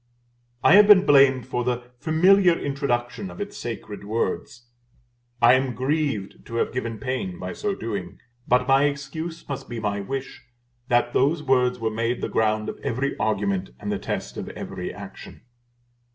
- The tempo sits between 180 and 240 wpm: No, average, 165 wpm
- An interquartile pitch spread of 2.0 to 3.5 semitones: No, average, 3.9 semitones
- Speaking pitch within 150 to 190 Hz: No, low, 125 Hz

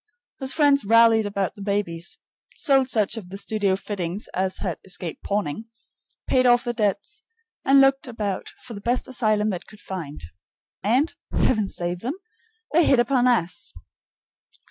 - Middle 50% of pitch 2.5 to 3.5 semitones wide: No, average, 4.7 semitones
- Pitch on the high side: Yes, high, 215 Hz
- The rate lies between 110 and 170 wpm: Yes, average, 155 wpm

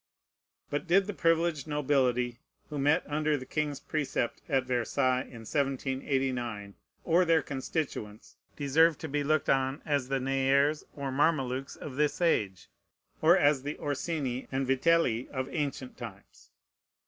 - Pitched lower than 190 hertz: Yes, medium, 140 Hz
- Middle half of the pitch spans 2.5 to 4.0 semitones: Yes, average, 2.9 semitones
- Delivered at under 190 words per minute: Yes, average, 140 wpm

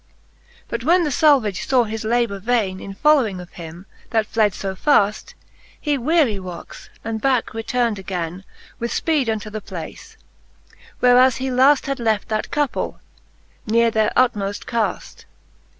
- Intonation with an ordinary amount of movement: Yes, average, 4.1 semitones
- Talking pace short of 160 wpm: Yes, average, 150 wpm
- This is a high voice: Yes, high, 225 Hz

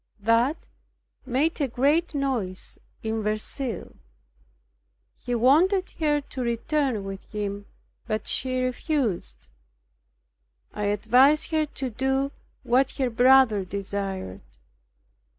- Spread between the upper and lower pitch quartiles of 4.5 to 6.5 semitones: Yes, average, 4.8 semitones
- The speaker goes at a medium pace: No, slow, 100 wpm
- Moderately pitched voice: No, very high, 250 Hz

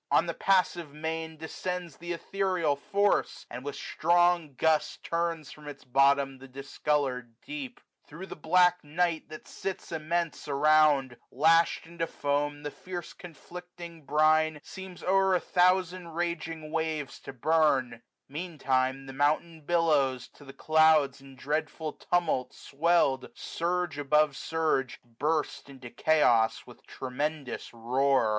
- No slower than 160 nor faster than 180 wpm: No, slow, 135 wpm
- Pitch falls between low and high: Yes, medium, 155 Hz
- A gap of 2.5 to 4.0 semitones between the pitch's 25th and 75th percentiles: Yes, average, 3.7 semitones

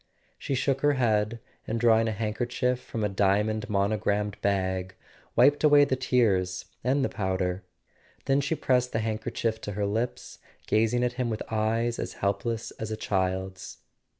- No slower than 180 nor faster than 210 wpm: No, average, 165 wpm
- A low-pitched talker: Yes, low, 110 Hz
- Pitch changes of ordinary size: Yes, average, 3.4 semitones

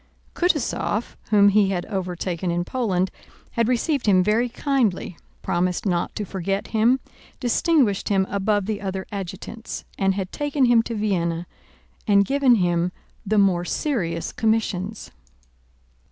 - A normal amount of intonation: Yes, average, 3.9 semitones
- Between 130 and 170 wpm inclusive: Yes, slow, 135 wpm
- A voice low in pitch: No, high, 200 Hz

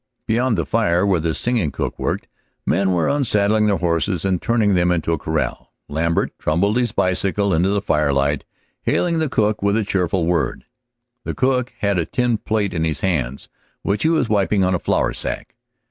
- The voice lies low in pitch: Yes, very low, 95 Hz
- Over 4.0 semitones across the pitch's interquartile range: Yes, average, 4.4 semitones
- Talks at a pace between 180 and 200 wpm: Yes, average, 190 wpm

